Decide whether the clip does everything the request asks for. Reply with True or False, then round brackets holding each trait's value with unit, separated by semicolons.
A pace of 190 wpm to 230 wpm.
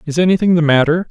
True (215 wpm)